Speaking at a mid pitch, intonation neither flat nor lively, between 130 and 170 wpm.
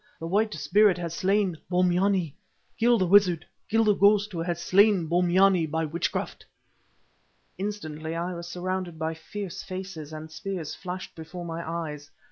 Yes: medium, 180 Hz; average, 3.2 semitones; average, 150 wpm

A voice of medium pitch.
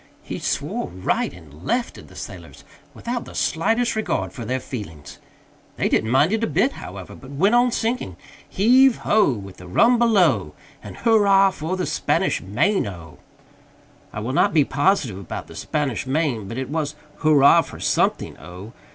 Yes: medium, 145 Hz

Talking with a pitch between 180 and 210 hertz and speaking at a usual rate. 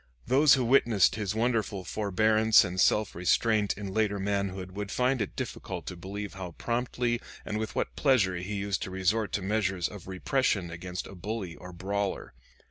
No: low, 100 Hz; average, 175 wpm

